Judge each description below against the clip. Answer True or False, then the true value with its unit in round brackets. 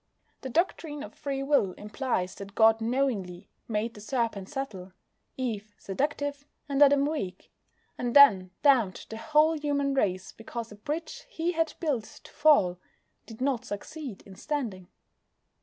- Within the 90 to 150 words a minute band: True (145 wpm)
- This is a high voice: True (250 Hz)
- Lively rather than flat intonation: True (5.8 semitones)